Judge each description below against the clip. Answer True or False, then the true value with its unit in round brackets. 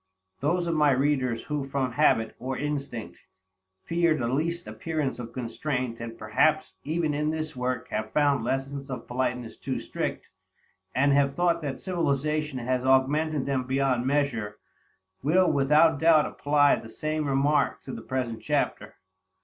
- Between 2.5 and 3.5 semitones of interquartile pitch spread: True (3.1 semitones)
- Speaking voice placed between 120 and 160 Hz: True (140 Hz)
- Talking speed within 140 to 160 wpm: True (155 wpm)